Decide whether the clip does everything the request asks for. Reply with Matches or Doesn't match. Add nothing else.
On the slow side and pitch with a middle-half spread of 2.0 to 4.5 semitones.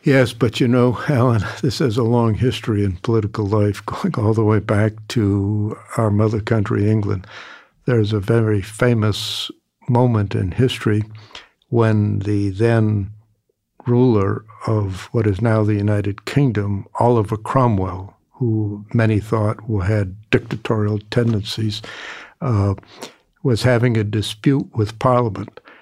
Matches